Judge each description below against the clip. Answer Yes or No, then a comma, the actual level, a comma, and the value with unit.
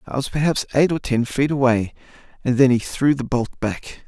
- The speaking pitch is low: Yes, low, 130 Hz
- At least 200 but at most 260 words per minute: Yes, fast, 205 wpm